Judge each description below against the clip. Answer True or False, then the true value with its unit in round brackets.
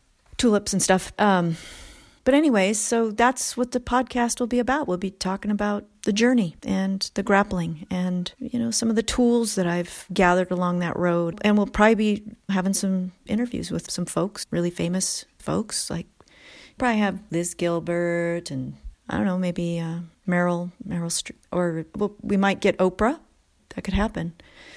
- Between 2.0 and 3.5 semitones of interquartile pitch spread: False (4.2 semitones)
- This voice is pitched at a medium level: False (195 Hz)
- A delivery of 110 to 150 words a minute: False (175 wpm)